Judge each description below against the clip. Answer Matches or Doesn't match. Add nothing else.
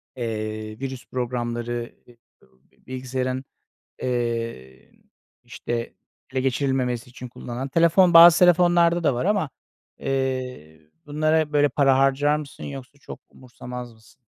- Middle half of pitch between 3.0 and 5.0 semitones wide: Matches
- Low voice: Matches